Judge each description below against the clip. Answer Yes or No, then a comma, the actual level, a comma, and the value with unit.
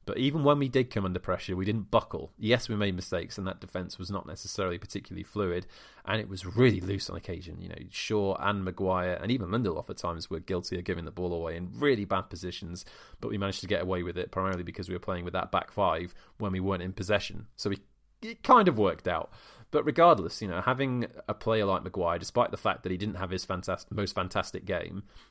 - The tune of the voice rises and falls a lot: No, average, 2.7 semitones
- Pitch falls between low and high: No, very low, 95 Hz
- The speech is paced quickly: Yes, fast, 240 wpm